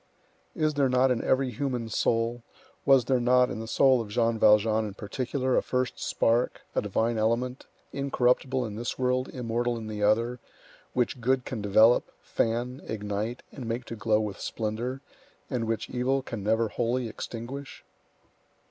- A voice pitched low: Yes, low, 120 Hz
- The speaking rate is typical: Yes, average, 165 wpm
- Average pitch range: No, narrow, 2.3 semitones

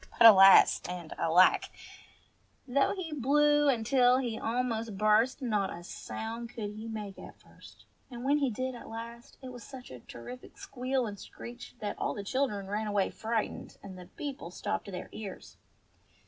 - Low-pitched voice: No, high, 225 Hz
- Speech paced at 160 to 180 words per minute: Yes, average, 170 wpm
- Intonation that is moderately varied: Yes, average, 3.7 semitones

